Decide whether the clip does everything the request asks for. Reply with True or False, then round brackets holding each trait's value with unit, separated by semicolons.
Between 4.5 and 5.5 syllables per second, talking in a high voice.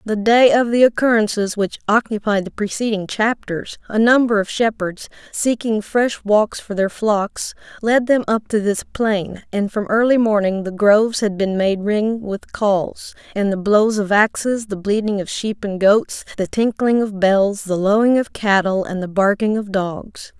False (4.3 syllables/s; 210 Hz)